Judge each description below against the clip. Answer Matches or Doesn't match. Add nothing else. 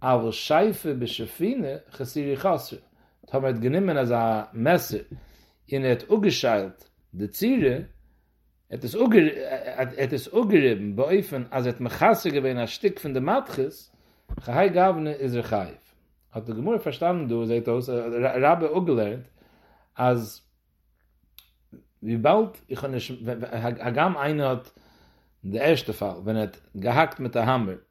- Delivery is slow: Matches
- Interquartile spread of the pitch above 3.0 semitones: Matches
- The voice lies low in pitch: Matches